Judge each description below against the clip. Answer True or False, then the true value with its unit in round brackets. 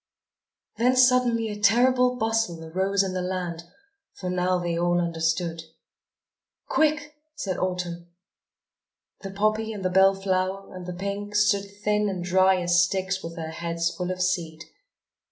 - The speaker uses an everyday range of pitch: True (3.0 semitones)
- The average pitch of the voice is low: False (185 Hz)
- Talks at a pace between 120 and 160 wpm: True (150 wpm)